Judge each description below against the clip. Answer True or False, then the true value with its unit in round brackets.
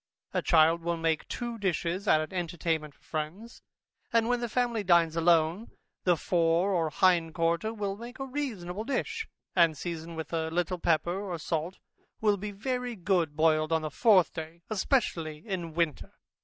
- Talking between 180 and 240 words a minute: False (170 wpm)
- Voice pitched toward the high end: False (175 Hz)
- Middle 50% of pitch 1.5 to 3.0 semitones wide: False (4.3 semitones)